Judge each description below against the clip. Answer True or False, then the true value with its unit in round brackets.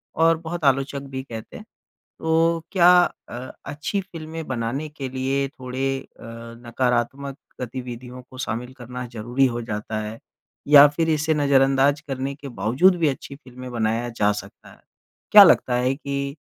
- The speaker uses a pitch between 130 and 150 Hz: True (135 Hz)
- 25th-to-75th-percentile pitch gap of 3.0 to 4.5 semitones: True (3.3 semitones)